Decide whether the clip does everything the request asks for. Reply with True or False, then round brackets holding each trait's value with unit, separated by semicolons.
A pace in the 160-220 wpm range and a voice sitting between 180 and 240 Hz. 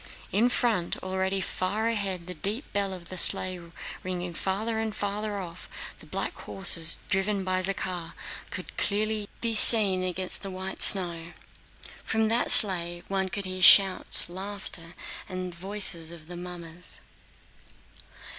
False (145 wpm; 190 Hz)